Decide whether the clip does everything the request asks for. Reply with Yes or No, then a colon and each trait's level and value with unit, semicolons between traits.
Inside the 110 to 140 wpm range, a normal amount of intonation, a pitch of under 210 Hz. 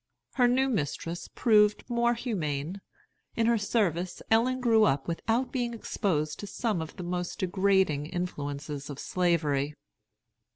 No: slow, 135 wpm; wide, 6.9 semitones; medium, 185 Hz